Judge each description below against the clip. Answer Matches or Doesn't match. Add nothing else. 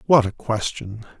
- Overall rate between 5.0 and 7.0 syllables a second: Doesn't match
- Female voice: Doesn't match